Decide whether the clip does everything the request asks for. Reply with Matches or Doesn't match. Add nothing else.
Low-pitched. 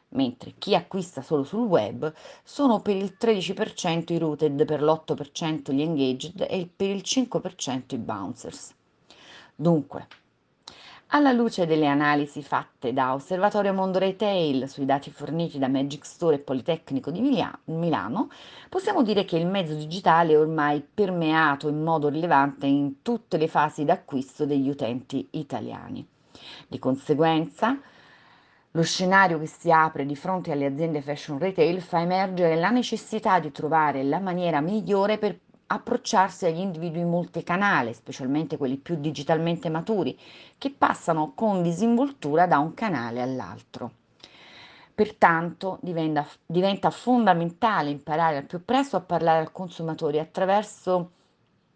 Doesn't match